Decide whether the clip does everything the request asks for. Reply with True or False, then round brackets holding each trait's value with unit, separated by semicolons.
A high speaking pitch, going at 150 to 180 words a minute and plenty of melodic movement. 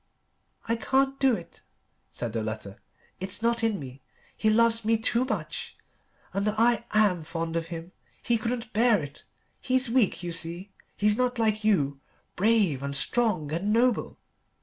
True (215 Hz; 160 wpm; 5.8 semitones)